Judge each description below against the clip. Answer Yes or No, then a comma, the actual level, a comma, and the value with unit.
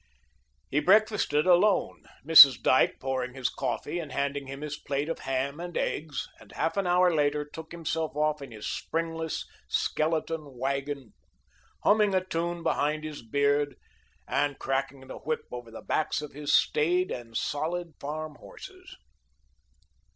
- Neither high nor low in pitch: Yes, medium, 150 Hz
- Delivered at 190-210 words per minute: No, average, 150 wpm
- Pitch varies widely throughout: No, average, 3.1 semitones